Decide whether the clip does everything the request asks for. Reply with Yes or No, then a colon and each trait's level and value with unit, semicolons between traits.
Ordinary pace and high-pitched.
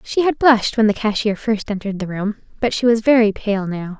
No: fast, 240 wpm; high, 215 Hz